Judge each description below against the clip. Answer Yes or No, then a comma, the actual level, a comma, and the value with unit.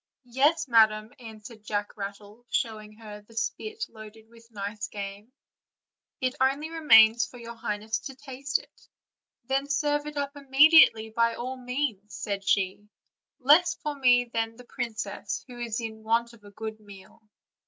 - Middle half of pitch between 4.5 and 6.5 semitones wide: No, average, 3.7 semitones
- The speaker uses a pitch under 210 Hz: No, high, 230 Hz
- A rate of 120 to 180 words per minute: Yes, average, 155 wpm